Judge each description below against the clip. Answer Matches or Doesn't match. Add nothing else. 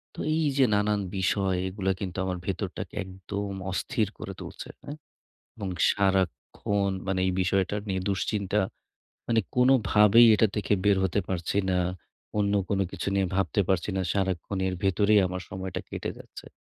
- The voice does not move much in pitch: Matches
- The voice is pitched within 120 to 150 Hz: Doesn't match